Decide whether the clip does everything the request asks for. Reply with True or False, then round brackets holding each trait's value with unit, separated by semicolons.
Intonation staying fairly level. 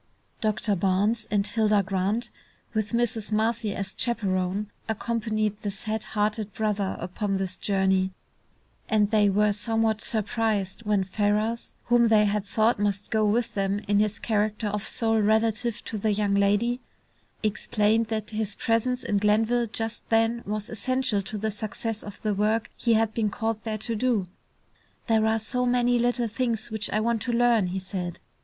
True (1.8 semitones)